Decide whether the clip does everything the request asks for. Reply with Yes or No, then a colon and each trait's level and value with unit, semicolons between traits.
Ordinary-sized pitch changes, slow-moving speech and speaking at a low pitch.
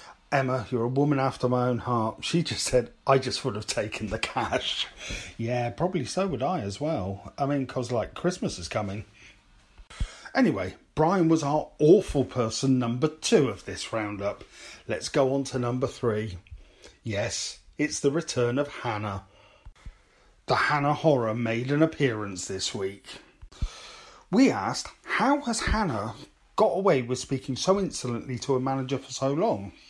No: average, 4.8 semitones; average, 160 wpm; low, 130 Hz